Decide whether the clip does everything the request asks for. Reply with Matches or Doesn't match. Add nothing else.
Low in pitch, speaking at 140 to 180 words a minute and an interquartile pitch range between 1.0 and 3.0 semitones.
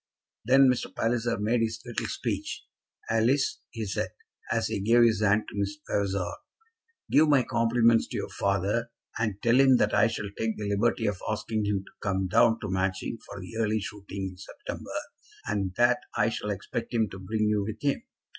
Doesn't match